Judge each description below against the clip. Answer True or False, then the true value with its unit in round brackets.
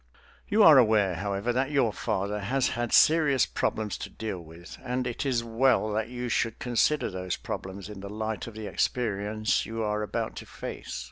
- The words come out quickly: False (190 wpm)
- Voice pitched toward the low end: True (110 Hz)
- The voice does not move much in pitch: False (3.4 semitones)